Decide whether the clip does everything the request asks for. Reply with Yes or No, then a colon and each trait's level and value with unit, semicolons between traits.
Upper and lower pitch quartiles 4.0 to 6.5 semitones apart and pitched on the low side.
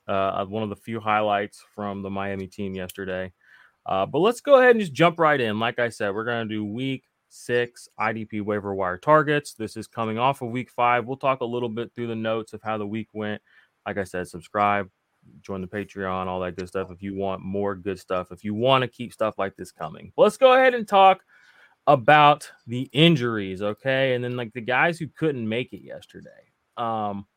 Yes: average, 4.4 semitones; low, 110 Hz